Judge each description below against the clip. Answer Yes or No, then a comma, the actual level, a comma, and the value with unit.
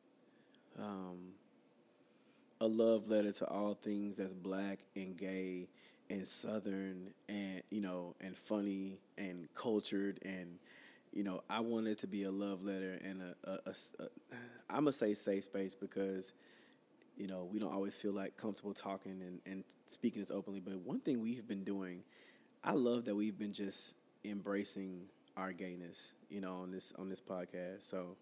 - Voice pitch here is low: Yes, very low, 95 Hz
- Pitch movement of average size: No, narrow, 1.5 semitones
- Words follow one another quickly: No, average, 170 wpm